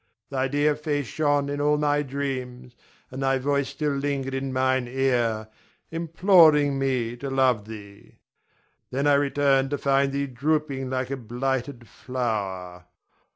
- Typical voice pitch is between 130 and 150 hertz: Yes, low, 135 Hz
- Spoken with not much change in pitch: Yes, narrow, 2.3 semitones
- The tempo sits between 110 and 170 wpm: Yes, average, 145 wpm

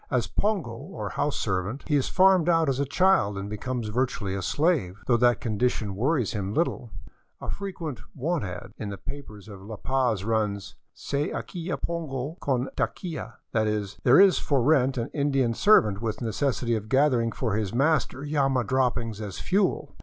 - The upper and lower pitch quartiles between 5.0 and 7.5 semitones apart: Yes, wide, 5.5 semitones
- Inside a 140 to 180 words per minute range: No, average, 190 wpm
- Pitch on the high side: No, low, 125 Hz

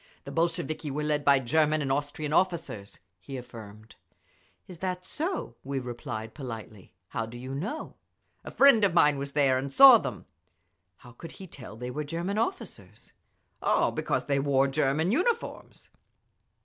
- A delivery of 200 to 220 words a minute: No, average, 160 wpm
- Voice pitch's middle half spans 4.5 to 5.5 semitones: Yes, average, 5.1 semitones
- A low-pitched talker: No, medium, 145 Hz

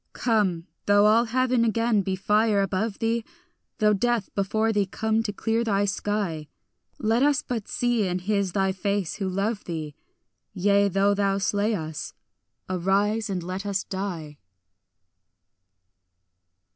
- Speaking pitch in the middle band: No, high, 205 Hz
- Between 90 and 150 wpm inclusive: Yes, average, 140 wpm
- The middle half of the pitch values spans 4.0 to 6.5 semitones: No, narrow, 2.6 semitones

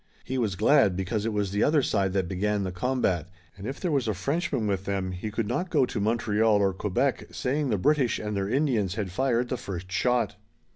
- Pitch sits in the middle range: No, low, 105 Hz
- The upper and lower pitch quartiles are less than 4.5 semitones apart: No, average, 4.8 semitones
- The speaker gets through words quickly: Yes, fast, 225 wpm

